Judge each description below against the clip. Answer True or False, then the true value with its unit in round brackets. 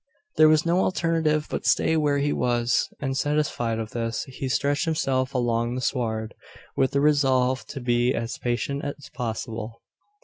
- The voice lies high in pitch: False (130 Hz)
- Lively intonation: False (3.5 semitones)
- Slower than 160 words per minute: False (165 wpm)